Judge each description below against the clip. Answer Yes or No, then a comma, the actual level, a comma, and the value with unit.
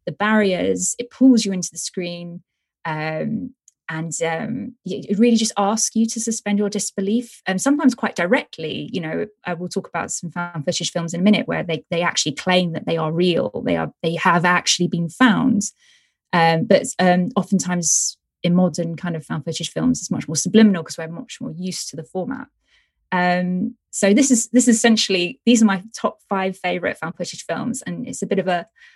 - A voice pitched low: No, medium, 185 Hz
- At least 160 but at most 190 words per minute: No, fast, 205 wpm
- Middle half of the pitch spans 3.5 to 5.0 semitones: Yes, average, 4.5 semitones